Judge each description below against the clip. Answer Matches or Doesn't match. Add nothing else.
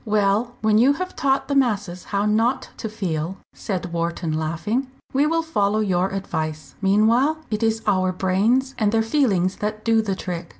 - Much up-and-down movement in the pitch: Doesn't match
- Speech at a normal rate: Matches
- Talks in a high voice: Matches